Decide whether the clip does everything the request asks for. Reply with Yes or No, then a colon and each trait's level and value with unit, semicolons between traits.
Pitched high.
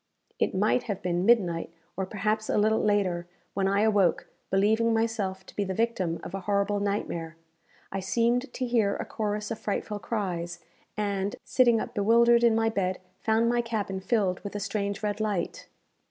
Yes: high, 205 Hz